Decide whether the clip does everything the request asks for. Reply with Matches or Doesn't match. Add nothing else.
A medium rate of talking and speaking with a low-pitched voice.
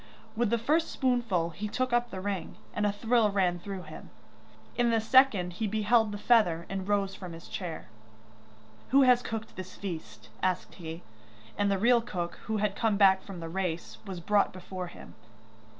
Doesn't match